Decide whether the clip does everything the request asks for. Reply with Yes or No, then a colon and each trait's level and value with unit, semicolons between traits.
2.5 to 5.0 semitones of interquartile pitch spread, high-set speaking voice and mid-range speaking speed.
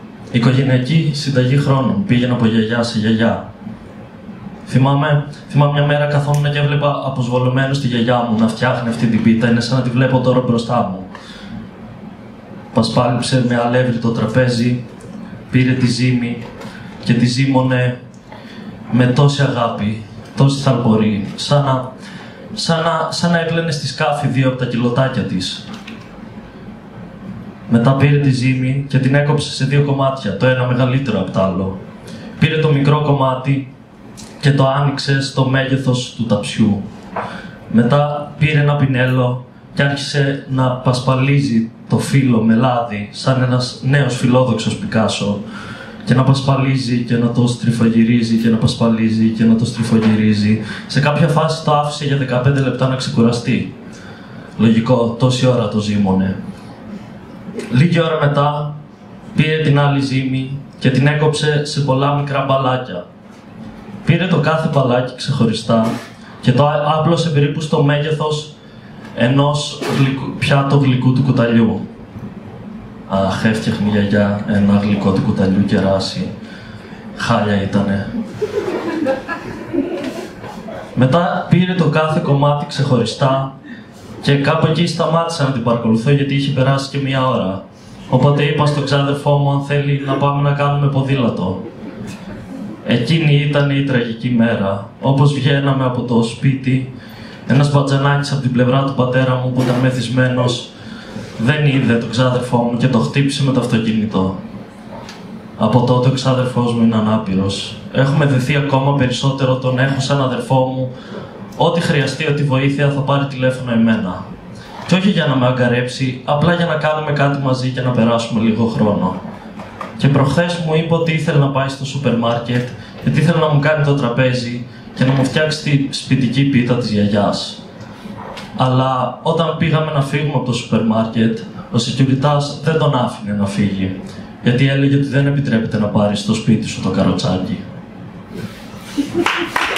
No: average, 3.3 semitones; low, 130 Hz; average, 145 wpm